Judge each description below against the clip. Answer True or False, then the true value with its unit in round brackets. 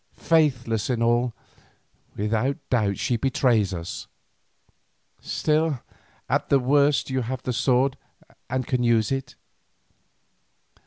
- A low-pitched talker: True (125 Hz)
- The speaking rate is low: True (110 wpm)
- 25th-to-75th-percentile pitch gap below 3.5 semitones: True (2.8 semitones)